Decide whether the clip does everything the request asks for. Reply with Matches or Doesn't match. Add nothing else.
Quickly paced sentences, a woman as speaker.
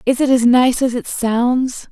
Matches